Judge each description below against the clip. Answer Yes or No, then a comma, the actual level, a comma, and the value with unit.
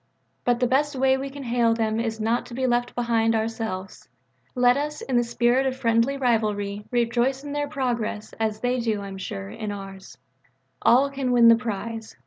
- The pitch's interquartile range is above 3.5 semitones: No, average, 2.7 semitones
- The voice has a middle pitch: No, high, 235 Hz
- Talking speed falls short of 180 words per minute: No, average, 195 wpm